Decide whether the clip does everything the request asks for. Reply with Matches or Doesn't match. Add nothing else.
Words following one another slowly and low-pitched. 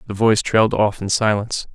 Doesn't match